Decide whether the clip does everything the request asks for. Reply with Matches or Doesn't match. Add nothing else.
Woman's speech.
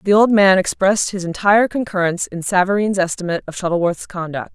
Matches